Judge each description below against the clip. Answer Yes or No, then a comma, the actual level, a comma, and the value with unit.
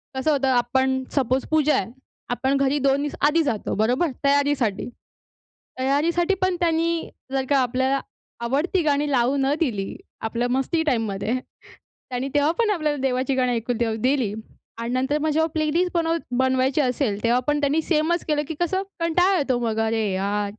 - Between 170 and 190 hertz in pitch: No, very high, 275 Hz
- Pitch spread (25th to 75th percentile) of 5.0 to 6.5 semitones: No, average, 4.0 semitones